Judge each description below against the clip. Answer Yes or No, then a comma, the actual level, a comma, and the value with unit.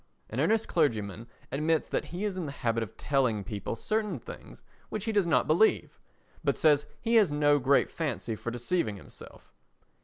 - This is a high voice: No, medium, 145 Hz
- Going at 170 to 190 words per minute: Yes, average, 180 wpm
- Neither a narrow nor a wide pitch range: No, wide, 7.8 semitones